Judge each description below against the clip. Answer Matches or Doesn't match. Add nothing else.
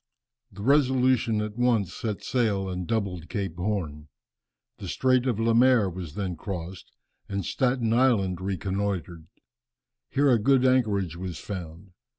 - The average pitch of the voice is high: Doesn't match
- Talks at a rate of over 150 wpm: Doesn't match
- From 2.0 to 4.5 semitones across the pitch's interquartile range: Doesn't match